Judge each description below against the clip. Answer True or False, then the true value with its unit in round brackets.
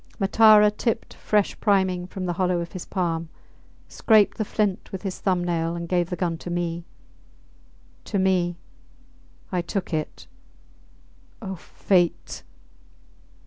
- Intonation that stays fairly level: True (2.3 semitones)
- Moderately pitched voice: True (180 Hz)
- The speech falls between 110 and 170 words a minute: True (135 wpm)